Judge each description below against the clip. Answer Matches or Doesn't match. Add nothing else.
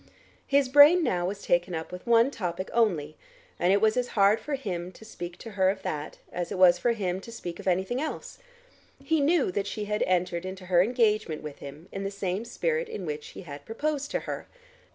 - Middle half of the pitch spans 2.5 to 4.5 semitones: Doesn't match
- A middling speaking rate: Doesn't match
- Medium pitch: Doesn't match